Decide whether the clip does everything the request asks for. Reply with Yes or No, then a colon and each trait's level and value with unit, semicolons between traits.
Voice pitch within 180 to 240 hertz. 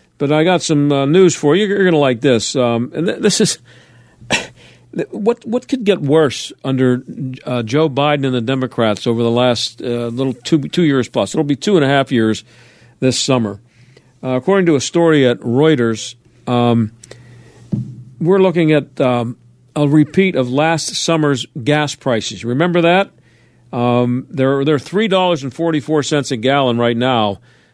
No: low, 135 Hz